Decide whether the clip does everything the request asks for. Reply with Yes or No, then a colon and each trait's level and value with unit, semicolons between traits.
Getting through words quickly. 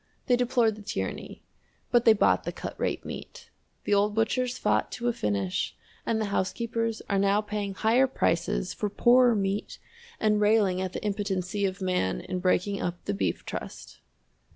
No: average, 175 wpm